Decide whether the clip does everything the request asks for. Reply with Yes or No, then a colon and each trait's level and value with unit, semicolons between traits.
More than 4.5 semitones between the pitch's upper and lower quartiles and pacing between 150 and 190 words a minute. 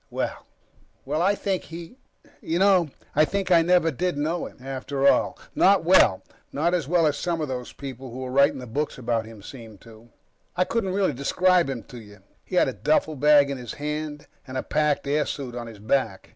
No: average, 4.9 semitones; average, 200 wpm